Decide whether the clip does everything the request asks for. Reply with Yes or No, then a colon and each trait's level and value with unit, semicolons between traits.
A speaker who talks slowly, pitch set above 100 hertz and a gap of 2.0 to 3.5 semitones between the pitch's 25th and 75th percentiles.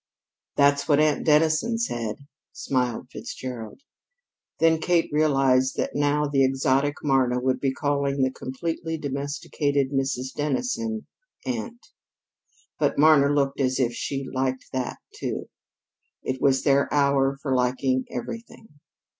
Yes: slow, 125 wpm; medium, 140 Hz; narrow, 2.5 semitones